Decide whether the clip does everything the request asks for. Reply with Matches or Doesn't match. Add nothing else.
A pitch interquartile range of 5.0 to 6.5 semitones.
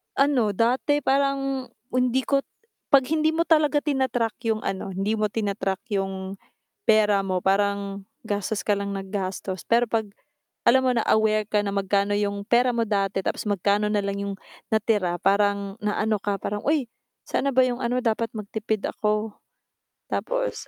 Doesn't match